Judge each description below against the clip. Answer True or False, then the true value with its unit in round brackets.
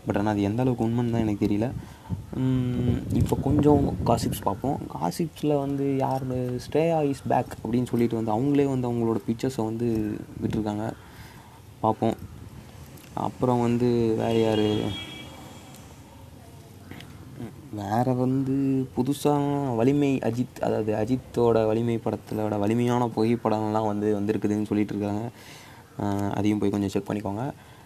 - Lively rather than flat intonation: False (3.3 semitones)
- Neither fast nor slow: True (115 wpm)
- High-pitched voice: False (115 Hz)